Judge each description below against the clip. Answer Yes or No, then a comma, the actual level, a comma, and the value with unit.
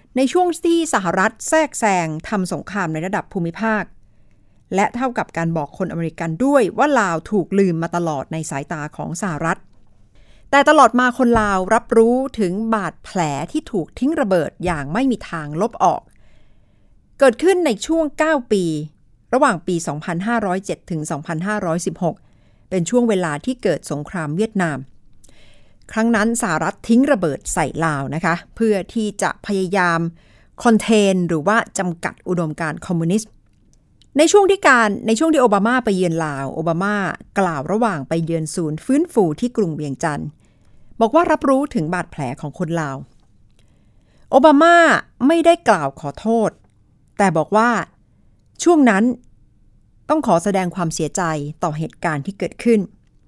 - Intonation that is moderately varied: No, wide, 6.4 semitones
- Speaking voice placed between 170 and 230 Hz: Yes, high, 190 Hz